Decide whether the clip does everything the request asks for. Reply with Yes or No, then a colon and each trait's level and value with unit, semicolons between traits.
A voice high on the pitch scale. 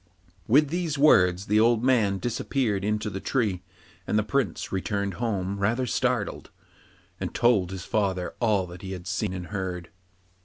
No: low, 105 Hz